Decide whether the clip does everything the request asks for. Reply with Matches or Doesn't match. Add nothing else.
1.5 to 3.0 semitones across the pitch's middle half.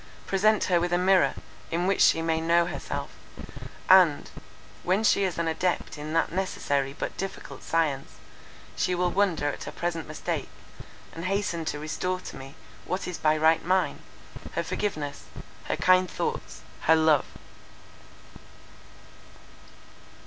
Matches